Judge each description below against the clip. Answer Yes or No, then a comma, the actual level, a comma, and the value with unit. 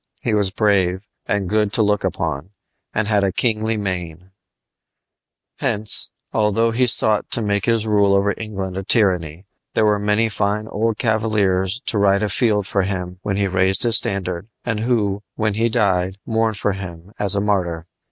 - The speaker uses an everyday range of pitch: No, narrow, 2.3 semitones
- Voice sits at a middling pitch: No, low, 100 Hz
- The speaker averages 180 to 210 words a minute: No, average, 170 wpm